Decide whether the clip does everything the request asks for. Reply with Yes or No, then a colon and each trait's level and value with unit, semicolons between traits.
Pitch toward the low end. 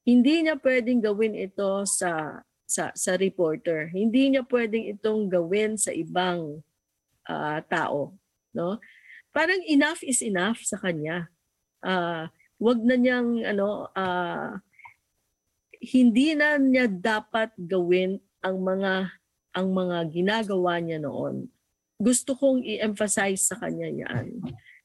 No: high, 205 Hz